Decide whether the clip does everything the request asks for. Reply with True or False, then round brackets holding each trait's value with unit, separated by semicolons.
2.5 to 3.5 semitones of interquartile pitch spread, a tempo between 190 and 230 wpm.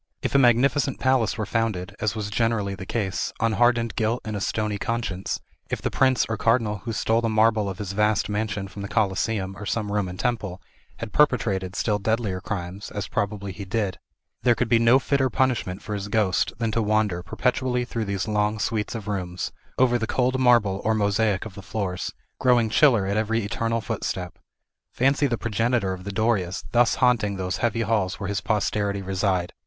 True (2.8 semitones; 195 wpm)